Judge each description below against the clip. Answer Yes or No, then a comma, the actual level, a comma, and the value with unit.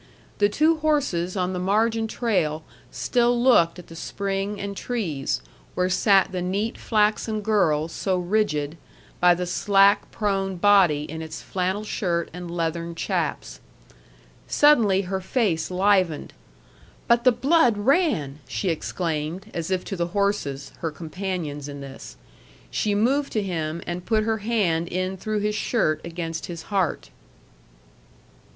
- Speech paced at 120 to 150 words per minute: Yes, average, 145 wpm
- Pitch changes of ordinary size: Yes, average, 4.1 semitones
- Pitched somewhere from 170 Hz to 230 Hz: Yes, high, 190 Hz